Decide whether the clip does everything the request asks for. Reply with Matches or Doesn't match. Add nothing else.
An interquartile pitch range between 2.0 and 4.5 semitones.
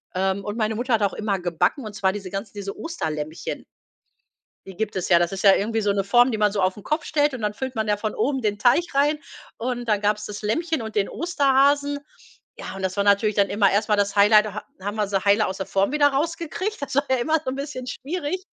Doesn't match